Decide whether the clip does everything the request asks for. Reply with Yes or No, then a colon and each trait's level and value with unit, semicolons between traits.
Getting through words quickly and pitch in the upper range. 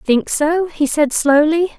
No: average, 170 wpm; very high, 305 Hz